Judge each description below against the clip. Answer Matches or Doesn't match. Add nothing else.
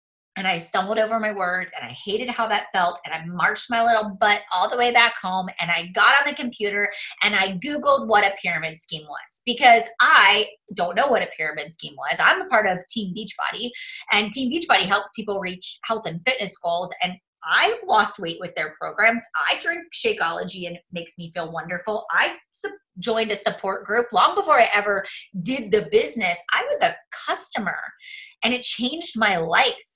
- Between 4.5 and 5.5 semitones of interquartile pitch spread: Matches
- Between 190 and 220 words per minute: Matches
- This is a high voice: Matches